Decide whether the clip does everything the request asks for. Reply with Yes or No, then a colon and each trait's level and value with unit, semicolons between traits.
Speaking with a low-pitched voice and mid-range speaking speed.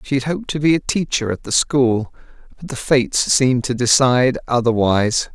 Yes: low, 130 Hz; average, 190 wpm